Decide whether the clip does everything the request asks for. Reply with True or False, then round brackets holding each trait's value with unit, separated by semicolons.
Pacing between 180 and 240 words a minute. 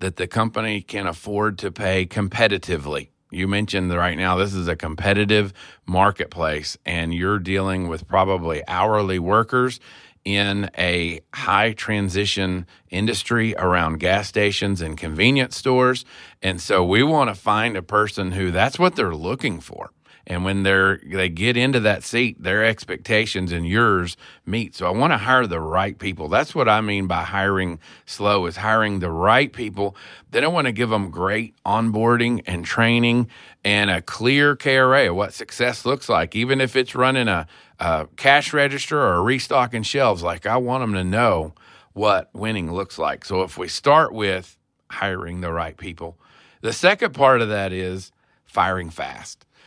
False (170 wpm)